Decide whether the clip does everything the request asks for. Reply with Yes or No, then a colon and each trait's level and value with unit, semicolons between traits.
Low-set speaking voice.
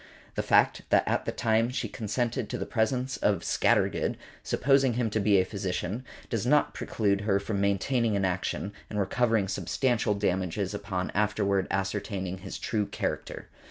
Yes: low, 105 Hz